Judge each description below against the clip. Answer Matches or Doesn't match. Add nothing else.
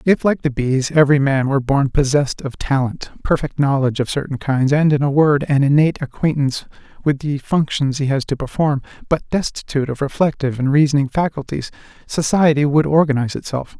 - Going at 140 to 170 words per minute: Doesn't match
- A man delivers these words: Matches